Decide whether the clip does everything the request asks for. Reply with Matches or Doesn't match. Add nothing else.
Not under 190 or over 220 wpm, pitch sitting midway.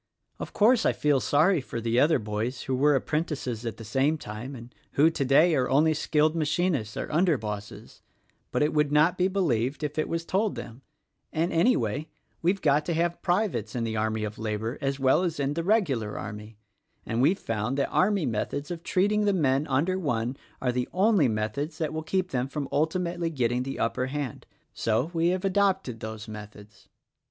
Matches